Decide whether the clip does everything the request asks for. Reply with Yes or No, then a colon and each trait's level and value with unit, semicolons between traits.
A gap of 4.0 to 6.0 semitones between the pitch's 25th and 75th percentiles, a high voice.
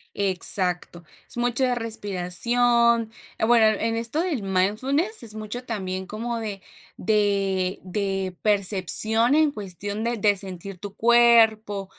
No: average, 3.5 semitones; high, 215 Hz